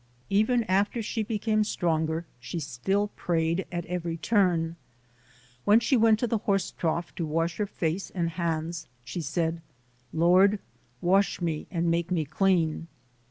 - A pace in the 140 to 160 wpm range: Yes, average, 150 wpm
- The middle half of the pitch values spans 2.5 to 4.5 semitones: Yes, average, 3.6 semitones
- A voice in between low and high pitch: Yes, medium, 175 Hz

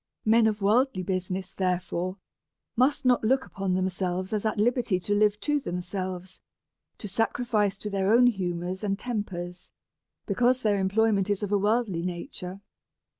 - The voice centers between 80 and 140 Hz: No, high, 200 Hz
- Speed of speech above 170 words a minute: No, average, 150 wpm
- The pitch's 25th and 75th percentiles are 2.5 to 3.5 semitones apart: Yes, average, 3.2 semitones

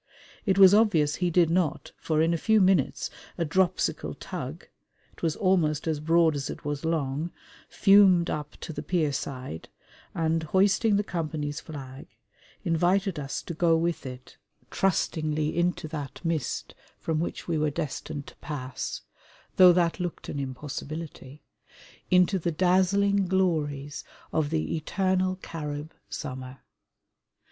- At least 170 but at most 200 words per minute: No, average, 140 wpm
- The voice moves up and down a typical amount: Yes, average, 3.6 semitones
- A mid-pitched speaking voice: Yes, medium, 165 Hz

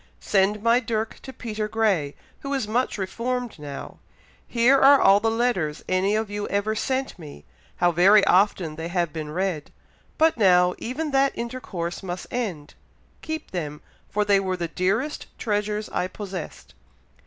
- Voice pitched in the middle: No, high, 205 Hz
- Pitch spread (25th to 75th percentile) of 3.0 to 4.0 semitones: No, average, 4.7 semitones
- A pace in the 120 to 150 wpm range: No, average, 160 wpm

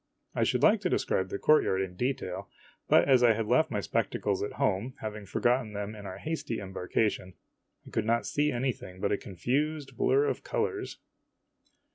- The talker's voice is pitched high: No, low, 115 Hz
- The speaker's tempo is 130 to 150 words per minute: No, average, 180 wpm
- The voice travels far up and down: Yes, wide, 6.5 semitones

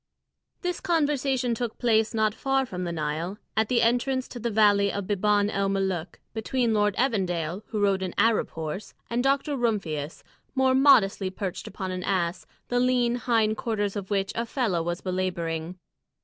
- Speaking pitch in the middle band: No, high, 210 Hz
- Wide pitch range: No, average, 4.6 semitones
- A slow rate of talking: No, average, 170 wpm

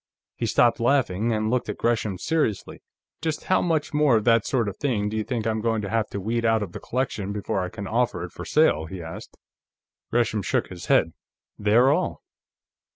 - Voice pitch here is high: No, low, 110 Hz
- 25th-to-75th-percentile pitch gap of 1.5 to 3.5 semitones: Yes, average, 3.0 semitones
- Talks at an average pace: No, fast, 210 wpm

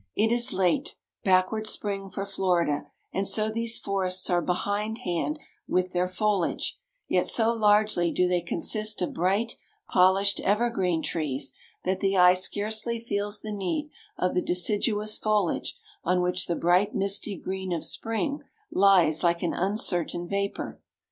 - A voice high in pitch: Yes, high, 195 Hz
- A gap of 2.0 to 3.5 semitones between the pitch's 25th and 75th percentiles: Yes, average, 3.0 semitones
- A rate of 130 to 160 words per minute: Yes, average, 150 wpm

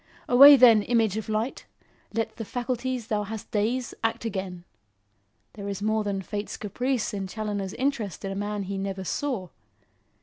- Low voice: No, high, 215 Hz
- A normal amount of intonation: Yes, average, 3.2 semitones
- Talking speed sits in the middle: Yes, average, 165 wpm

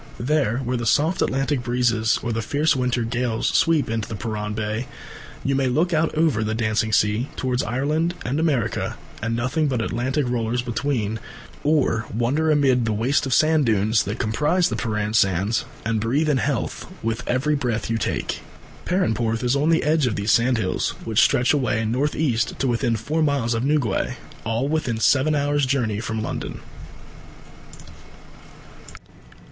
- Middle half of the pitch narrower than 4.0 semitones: No, average, 4.3 semitones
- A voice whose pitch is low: Yes, low, 120 Hz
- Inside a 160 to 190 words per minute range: Yes, average, 165 wpm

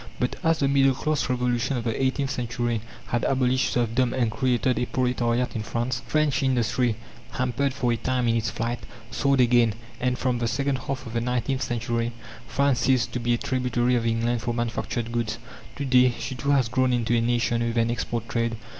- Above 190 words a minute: Yes, average, 200 wpm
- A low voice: Yes, low, 120 Hz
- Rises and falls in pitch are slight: Yes, narrow, 1.7 semitones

